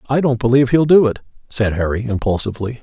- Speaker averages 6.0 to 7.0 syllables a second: Yes, 6.9 syllables/s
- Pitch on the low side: Yes, low, 120 Hz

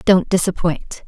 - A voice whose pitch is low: No, medium, 180 Hz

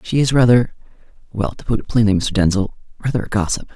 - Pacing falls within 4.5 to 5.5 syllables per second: No, 6.3 syllables/s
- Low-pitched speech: Yes, low, 110 Hz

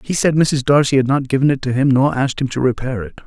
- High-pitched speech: No, low, 135 Hz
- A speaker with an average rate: No, fast, 295 wpm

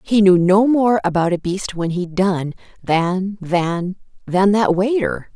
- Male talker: No, female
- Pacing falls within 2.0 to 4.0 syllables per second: Yes, 3.7 syllables/s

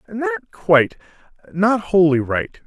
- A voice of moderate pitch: Yes, medium, 170 Hz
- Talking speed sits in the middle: No, slow, 115 wpm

